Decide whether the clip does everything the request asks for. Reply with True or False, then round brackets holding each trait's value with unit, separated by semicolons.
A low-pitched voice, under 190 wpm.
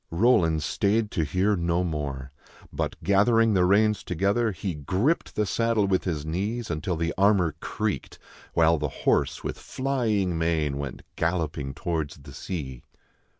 True (90 Hz; 150 wpm)